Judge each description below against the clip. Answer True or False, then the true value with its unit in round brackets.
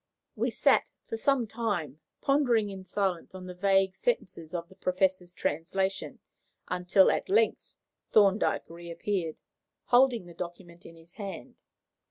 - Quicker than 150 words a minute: False (135 wpm)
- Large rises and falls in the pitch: False (3.3 semitones)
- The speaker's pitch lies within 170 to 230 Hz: True (190 Hz)